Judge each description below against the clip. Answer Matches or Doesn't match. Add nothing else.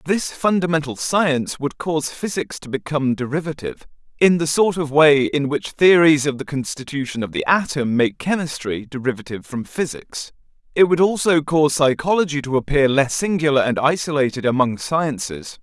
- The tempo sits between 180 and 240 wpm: Doesn't match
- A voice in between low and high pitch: Matches